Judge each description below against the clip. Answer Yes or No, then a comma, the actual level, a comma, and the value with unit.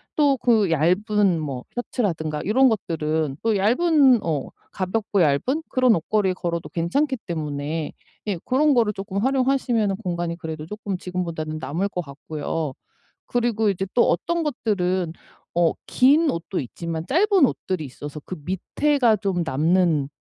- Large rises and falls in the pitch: Yes, wide, 6.7 semitones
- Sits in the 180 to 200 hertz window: Yes, high, 190 Hz